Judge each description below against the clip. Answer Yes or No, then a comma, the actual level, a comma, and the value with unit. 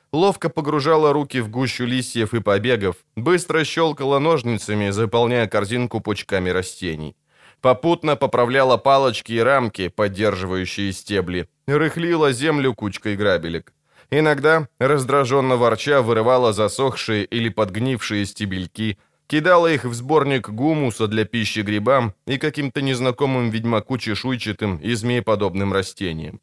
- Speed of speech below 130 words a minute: Yes, average, 110 wpm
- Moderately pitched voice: No, low, 120 Hz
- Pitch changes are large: No, average, 4.8 semitones